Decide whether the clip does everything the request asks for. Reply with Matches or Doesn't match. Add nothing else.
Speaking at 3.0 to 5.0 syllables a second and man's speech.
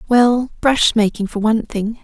Doesn't match